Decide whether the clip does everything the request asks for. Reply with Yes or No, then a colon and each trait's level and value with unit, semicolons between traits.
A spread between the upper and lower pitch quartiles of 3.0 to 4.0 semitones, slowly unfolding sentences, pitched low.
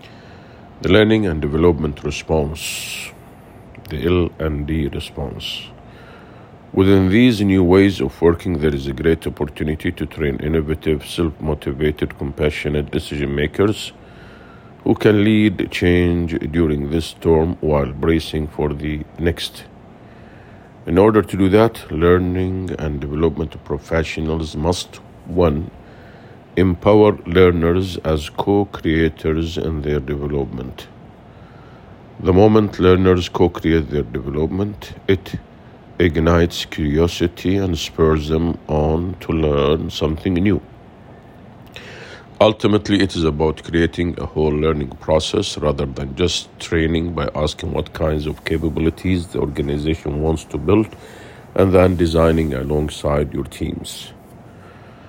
Yes: average, 3.6 semitones; slow, 115 wpm; very low, 80 Hz